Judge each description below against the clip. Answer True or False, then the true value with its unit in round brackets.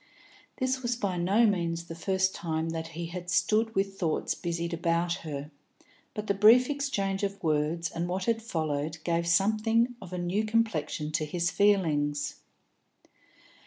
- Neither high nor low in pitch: True (180 Hz)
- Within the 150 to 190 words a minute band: True (160 wpm)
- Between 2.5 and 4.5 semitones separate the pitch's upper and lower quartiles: True (4.1 semitones)